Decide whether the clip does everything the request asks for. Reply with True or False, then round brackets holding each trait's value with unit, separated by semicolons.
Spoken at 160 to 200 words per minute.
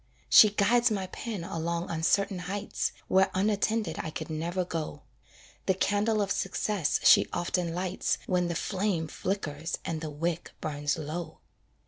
False (145 wpm)